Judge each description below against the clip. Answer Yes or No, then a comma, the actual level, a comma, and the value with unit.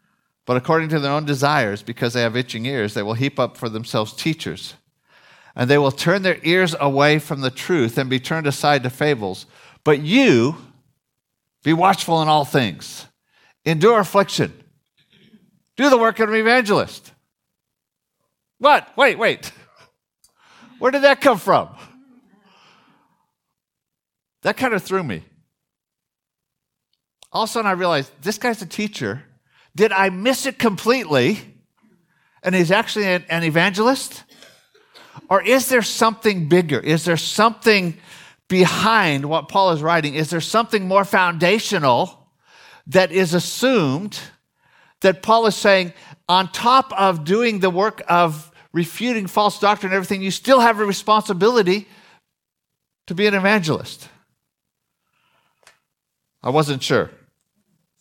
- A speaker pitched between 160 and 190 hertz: Yes, medium, 185 Hz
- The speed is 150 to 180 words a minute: No, slow, 135 wpm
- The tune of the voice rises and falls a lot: Yes, wide, 6.2 semitones